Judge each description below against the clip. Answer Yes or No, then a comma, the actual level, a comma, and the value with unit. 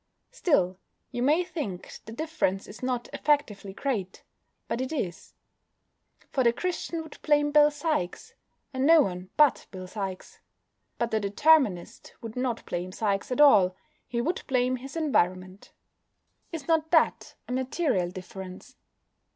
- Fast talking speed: No, average, 145 wpm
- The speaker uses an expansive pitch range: Yes, wide, 7.6 semitones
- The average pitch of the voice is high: Yes, very high, 250 Hz